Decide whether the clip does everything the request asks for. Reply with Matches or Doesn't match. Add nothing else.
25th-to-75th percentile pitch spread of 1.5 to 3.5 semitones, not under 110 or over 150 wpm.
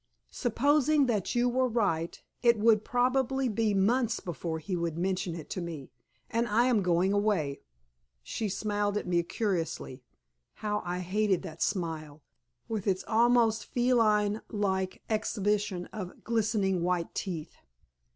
Doesn't match